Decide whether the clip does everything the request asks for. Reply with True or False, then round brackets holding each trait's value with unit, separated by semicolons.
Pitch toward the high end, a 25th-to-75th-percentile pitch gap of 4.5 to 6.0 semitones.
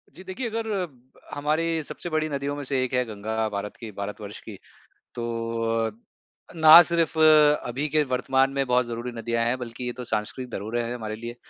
False (125 Hz; 4.8 semitones)